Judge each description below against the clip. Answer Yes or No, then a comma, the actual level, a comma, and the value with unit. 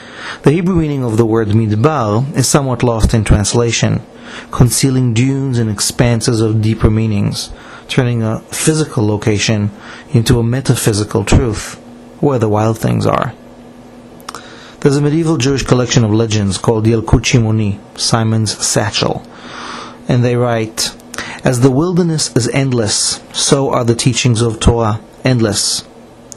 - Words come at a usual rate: No, slow, 130 wpm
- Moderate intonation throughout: Yes, average, 3.0 semitones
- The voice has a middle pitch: No, low, 115 Hz